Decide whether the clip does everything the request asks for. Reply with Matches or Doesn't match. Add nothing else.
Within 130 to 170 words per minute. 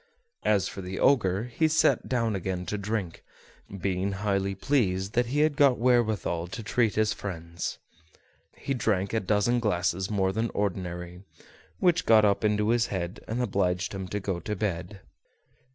Matches